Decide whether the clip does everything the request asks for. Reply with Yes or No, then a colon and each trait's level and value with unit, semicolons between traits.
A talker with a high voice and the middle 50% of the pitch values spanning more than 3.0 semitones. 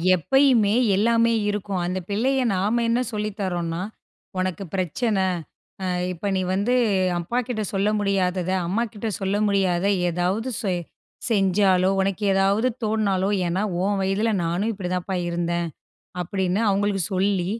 No: high, 195 Hz; narrow, 2.5 semitones